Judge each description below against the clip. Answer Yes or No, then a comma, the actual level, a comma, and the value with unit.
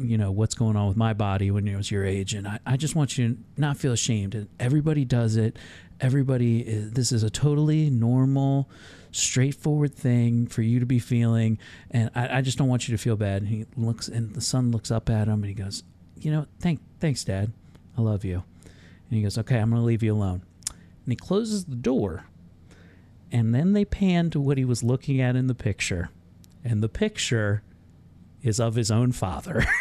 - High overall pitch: No, low, 115 Hz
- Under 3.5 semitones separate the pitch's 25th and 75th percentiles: No, average, 4.2 semitones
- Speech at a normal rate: No, fast, 215 wpm